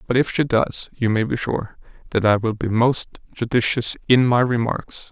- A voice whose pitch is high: No, low, 120 Hz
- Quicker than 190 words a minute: Yes, average, 200 wpm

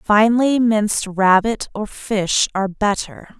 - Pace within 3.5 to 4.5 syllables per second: Yes, 4.0 syllables/s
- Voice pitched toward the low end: No, high, 210 Hz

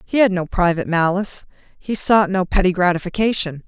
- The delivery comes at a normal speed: Yes, average, 145 wpm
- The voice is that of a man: No, female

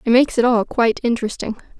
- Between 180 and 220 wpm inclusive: Yes, average, 200 wpm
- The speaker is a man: No, female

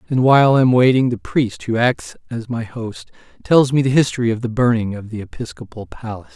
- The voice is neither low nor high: No, low, 120 Hz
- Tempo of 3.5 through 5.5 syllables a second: No, 5.8 syllables/s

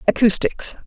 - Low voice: No, high, 215 Hz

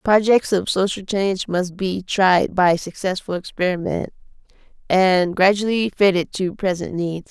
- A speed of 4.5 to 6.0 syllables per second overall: No, 4.3 syllables/s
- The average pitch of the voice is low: No, high, 190 Hz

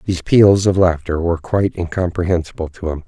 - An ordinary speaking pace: Yes, average, 175 wpm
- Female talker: No, male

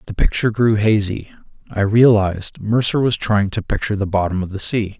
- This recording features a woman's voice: No, male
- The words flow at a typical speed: Yes, average, 190 wpm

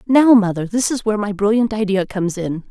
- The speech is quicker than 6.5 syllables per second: No, 6.0 syllables/s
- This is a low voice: No, high, 210 Hz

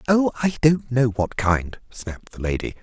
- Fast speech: No, average, 190 wpm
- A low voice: Yes, low, 125 Hz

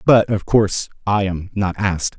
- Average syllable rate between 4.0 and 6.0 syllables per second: Yes, 4.8 syllables/s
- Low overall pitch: Yes, low, 100 Hz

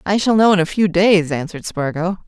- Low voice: No, medium, 180 Hz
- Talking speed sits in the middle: No, fast, 235 wpm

